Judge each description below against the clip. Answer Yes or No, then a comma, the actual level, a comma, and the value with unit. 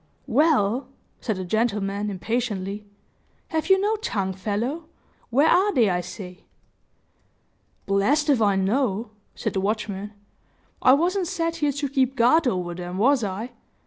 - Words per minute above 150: No, average, 145 wpm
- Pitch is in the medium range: No, high, 225 Hz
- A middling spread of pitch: No, wide, 6.6 semitones